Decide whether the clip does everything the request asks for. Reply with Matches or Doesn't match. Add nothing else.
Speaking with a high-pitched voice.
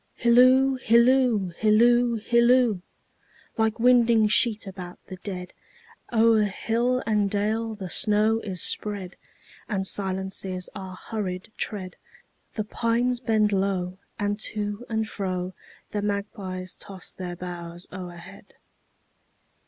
Matches